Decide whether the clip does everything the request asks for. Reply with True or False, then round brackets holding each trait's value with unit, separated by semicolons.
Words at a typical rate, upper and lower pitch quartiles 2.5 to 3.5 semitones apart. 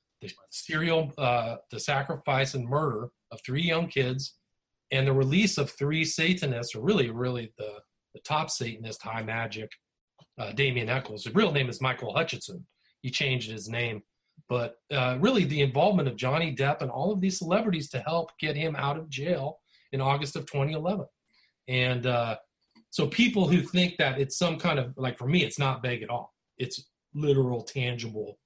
False (180 wpm; 4.5 semitones)